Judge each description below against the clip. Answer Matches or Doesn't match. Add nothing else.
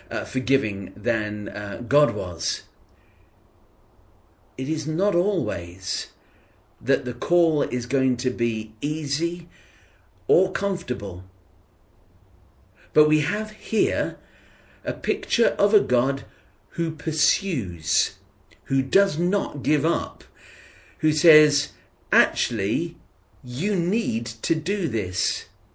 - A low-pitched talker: Matches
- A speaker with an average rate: Doesn't match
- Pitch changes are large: Matches